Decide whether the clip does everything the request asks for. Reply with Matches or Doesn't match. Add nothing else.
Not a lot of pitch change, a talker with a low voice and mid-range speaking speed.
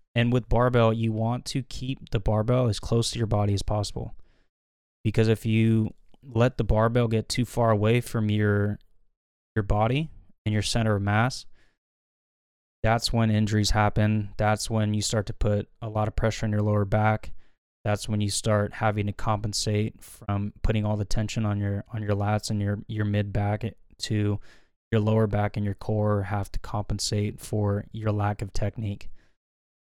Matches